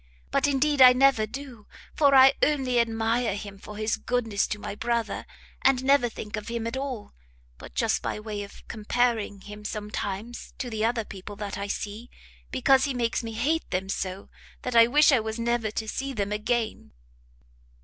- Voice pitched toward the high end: Yes, high, 230 Hz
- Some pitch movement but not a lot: Yes, average, 3.3 semitones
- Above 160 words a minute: Yes, average, 185 wpm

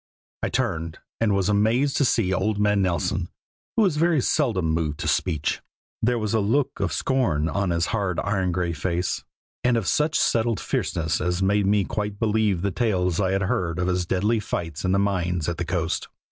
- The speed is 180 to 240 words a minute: Yes, average, 200 wpm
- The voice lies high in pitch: No, very low, 95 Hz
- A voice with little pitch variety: No, average, 3.9 semitones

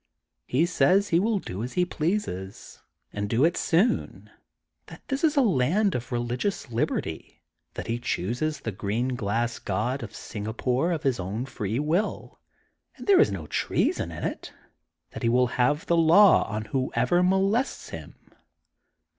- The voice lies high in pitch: No, low, 130 Hz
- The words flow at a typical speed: Yes, average, 160 wpm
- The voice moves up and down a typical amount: No, wide, 7.6 semitones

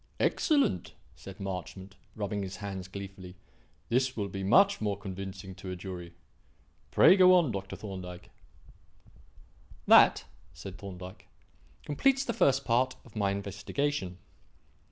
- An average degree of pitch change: Yes, average, 4.8 semitones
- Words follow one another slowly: Yes, slow, 125 wpm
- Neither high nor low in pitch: No, low, 100 Hz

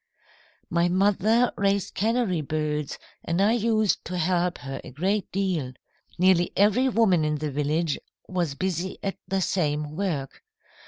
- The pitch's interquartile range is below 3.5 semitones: No, average, 4.6 semitones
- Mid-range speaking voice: Yes, medium, 180 Hz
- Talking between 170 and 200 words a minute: No, average, 145 wpm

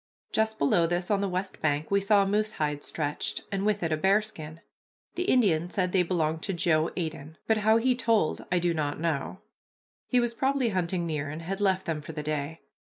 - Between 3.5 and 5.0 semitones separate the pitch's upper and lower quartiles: Yes, average, 4.7 semitones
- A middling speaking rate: No, fast, 215 wpm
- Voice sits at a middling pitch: Yes, medium, 180 Hz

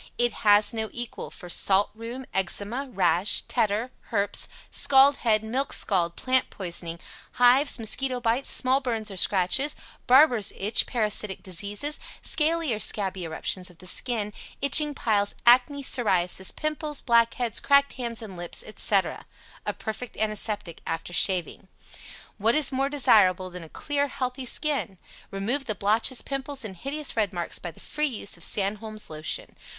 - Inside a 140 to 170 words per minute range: Yes, average, 150 wpm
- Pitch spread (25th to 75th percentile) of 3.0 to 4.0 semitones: No, average, 5.2 semitones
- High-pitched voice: Yes, high, 220 Hz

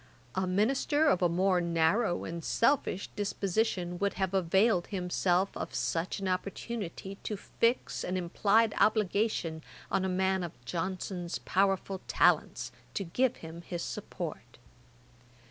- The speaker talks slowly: Yes, slow, 130 wpm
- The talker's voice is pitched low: No, high, 190 Hz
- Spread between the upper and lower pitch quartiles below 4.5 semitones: Yes, average, 2.7 semitones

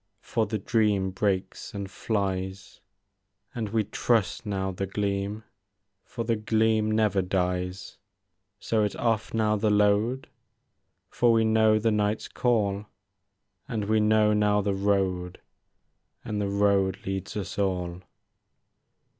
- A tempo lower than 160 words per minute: Yes, slow, 135 wpm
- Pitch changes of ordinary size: No, narrow, 2.1 semitones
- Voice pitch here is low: Yes, low, 105 Hz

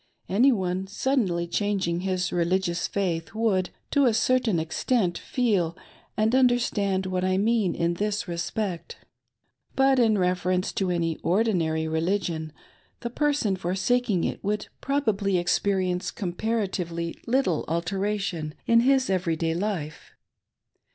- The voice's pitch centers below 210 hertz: Yes, high, 190 Hz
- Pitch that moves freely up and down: No, average, 4.2 semitones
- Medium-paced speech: No, slow, 125 wpm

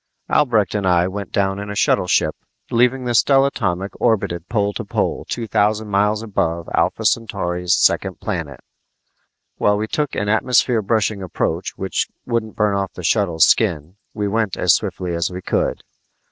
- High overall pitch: No, low, 100 Hz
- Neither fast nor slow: Yes, average, 160 wpm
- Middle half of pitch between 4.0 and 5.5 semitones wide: No, average, 3.6 semitones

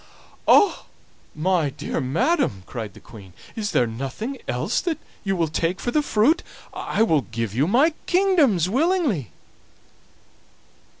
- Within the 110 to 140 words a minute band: Yes, slow, 135 wpm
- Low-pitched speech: No, medium, 185 Hz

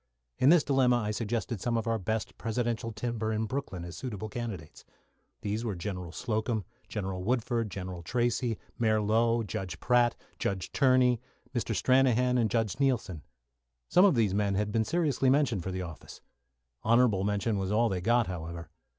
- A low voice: Yes, low, 110 Hz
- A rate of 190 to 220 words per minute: No, average, 170 wpm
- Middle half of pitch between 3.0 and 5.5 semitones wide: Yes, average, 3.6 semitones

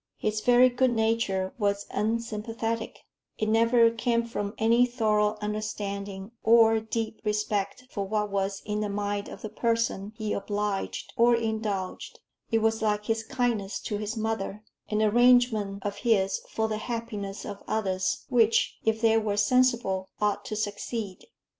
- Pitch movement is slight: Yes, narrow, 2.0 semitones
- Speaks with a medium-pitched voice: No, high, 215 Hz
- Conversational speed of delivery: Yes, average, 150 wpm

